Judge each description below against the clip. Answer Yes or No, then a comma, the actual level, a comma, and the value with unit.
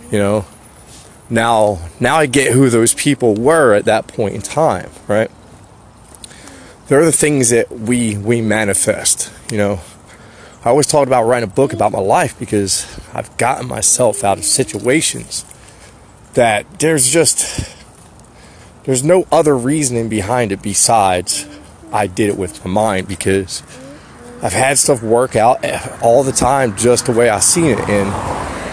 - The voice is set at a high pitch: No, low, 115 Hz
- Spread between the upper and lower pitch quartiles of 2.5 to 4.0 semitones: No, average, 4.6 semitones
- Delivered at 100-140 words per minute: No, average, 155 wpm